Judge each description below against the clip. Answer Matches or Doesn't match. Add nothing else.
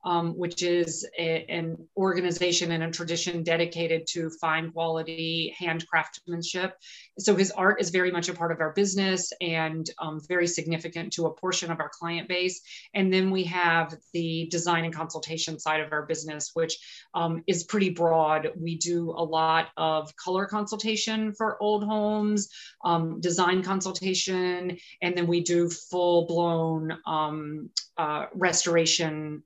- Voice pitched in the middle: Matches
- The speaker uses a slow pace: Doesn't match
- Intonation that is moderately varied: Doesn't match